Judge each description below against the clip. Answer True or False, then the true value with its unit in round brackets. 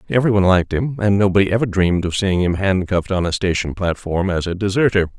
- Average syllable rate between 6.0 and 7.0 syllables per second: True (6.5 syllables/s)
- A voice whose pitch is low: True (95 Hz)